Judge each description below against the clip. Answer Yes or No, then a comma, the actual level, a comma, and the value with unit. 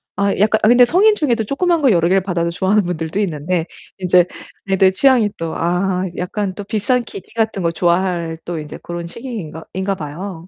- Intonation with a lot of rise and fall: No, average, 4.2 semitones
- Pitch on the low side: No, high, 190 Hz